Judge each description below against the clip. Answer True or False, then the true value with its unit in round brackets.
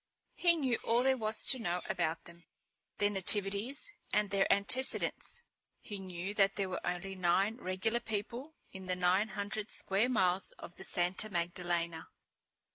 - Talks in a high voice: True (195 Hz)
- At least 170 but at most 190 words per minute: False (155 wpm)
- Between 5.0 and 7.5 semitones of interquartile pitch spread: False (3.5 semitones)